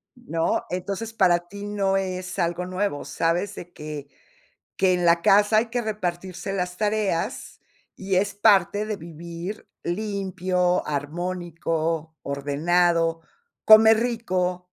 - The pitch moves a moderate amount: Yes, average, 3.2 semitones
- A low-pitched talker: No, medium, 185 Hz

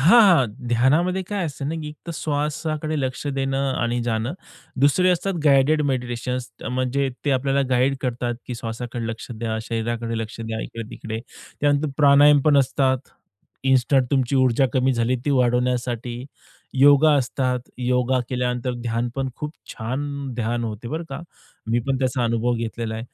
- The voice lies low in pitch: Yes, low, 130 Hz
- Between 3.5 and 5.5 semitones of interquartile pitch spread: No, average, 2.9 semitones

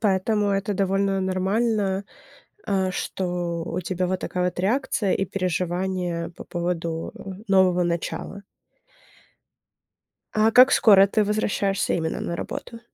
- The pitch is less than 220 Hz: Yes, high, 190 Hz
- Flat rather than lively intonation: Yes, narrow, 2.1 semitones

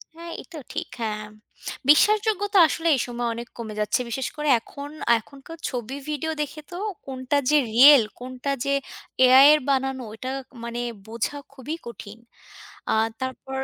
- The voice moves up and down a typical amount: Yes, average, 4.0 semitones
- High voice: Yes, very high, 265 Hz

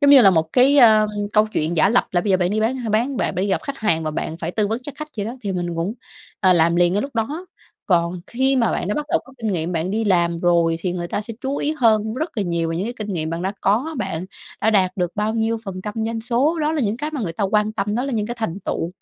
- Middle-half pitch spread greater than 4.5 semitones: Yes, average, 5.3 semitones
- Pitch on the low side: No, high, 210 Hz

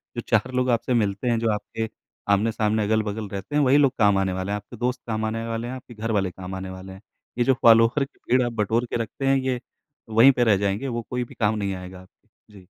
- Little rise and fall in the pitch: No, average, 3.3 semitones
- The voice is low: Yes, low, 110 Hz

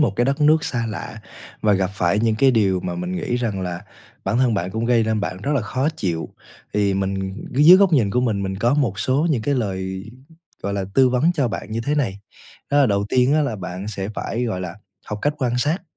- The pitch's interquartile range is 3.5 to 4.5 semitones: No, average, 5.2 semitones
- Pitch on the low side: Yes, low, 110 Hz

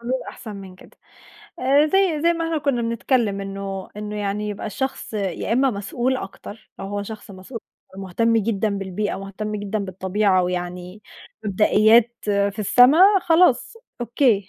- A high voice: Yes, high, 210 Hz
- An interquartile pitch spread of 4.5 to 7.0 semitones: No, average, 3.7 semitones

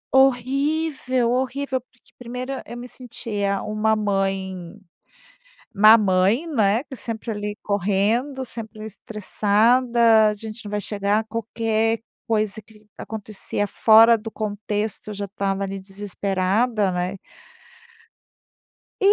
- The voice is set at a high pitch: Yes, high, 215 Hz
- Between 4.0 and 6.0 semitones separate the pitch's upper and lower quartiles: No, average, 2.9 semitones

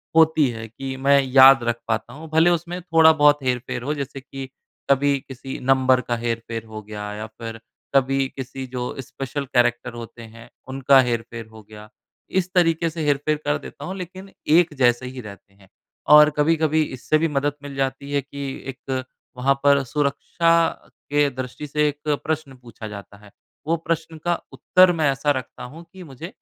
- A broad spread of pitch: No, average, 3.9 semitones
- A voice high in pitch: No, low, 135 Hz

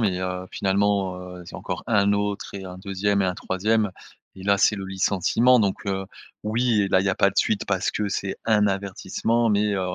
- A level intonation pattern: Yes, narrow, 1.6 semitones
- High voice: No, low, 100 Hz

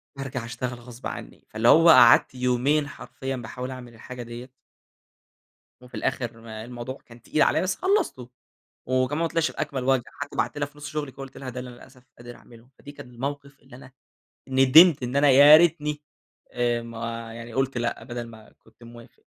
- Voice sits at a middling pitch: No, low, 125 Hz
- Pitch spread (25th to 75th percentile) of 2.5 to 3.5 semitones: Yes, average, 3.0 semitones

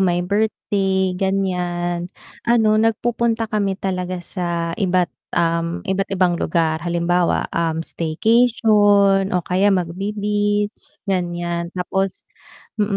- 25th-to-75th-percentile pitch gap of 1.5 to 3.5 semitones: Yes, average, 2.9 semitones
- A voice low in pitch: No, high, 190 Hz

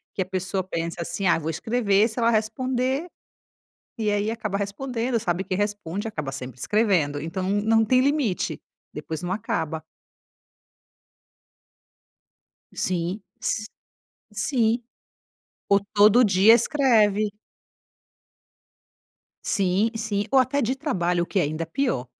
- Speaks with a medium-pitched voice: No, high, 205 Hz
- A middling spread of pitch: Yes, average, 4.4 semitones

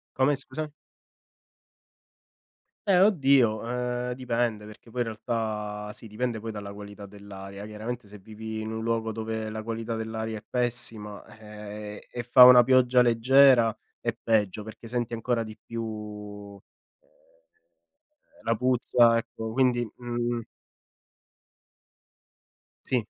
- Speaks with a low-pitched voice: Yes, low, 115 Hz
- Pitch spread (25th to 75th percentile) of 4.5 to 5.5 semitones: No, narrow, 2.4 semitones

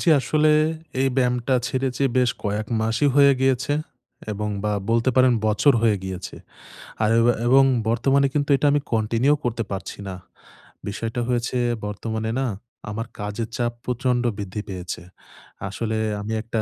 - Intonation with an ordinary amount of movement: Yes, average, 3.4 semitones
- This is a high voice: No, low, 115 Hz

